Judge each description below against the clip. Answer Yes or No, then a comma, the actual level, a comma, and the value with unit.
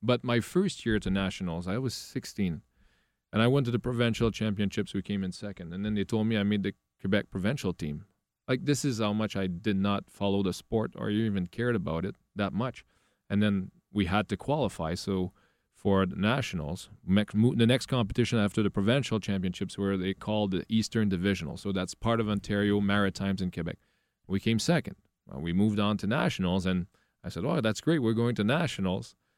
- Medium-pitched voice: No, low, 100 Hz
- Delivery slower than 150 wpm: No, fast, 205 wpm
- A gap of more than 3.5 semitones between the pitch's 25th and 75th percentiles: No, average, 2.7 semitones